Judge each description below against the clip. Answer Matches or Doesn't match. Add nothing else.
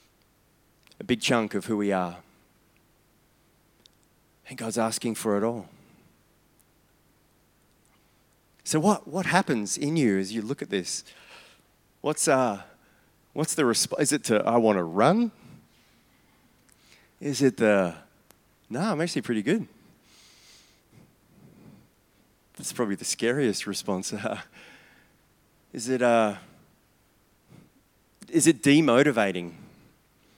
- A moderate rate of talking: Doesn't match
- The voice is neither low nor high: Doesn't match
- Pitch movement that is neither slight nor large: Doesn't match